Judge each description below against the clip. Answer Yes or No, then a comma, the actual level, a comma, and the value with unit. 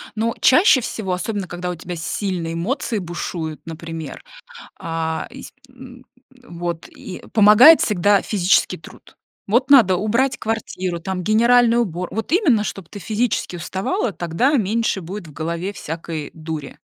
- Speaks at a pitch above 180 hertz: Yes, high, 190 Hz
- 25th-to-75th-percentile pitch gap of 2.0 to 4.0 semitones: No, average, 5.3 semitones